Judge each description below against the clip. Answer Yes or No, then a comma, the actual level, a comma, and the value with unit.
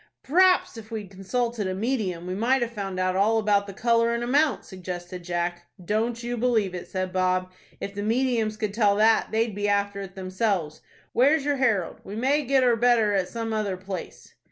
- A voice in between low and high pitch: No, high, 210 Hz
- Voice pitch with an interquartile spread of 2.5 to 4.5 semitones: Yes, average, 4.0 semitones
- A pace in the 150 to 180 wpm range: No, average, 200 wpm